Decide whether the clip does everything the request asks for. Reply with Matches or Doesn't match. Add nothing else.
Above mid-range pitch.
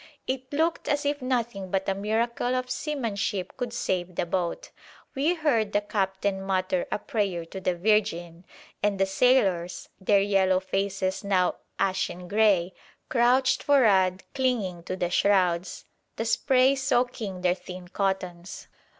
Matches